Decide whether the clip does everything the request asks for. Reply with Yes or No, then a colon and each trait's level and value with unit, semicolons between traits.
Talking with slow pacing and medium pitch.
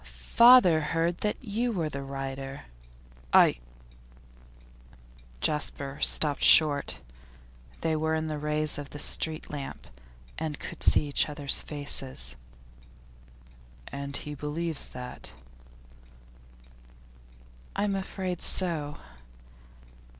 Yes: slow, 100 wpm; medium, 150 Hz